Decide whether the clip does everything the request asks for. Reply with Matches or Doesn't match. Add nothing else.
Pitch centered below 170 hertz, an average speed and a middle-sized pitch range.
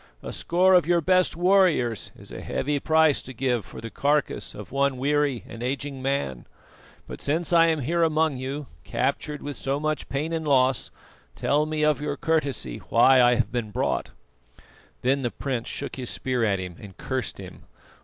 Matches